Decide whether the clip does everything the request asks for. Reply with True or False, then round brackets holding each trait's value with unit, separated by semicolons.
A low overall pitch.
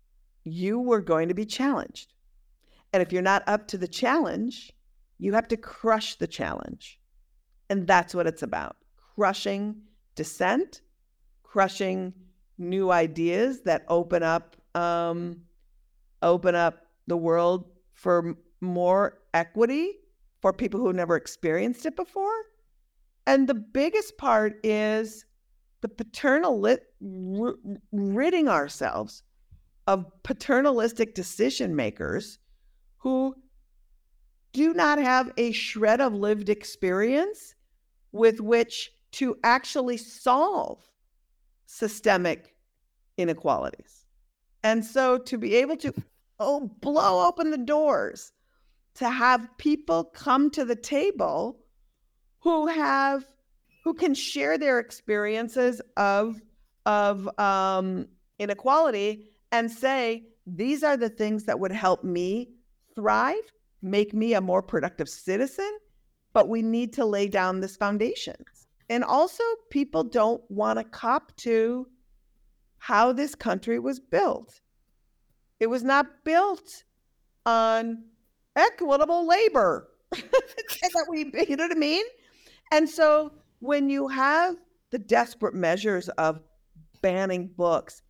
False (230 Hz)